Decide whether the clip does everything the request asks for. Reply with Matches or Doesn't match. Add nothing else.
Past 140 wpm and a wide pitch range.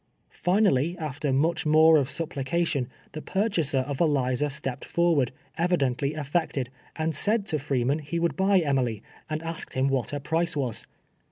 Doesn't match